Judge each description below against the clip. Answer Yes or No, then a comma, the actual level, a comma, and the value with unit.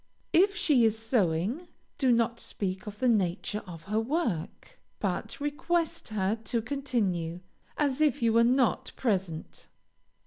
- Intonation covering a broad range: Yes, wide, 6.1 semitones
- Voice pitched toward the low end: No, high, 230 Hz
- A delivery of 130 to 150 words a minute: Yes, average, 140 wpm